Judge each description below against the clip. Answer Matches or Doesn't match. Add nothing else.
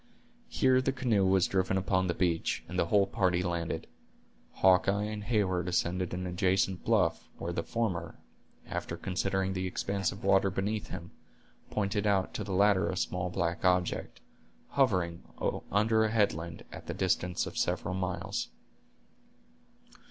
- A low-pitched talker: Matches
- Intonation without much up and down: Matches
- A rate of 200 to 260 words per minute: Doesn't match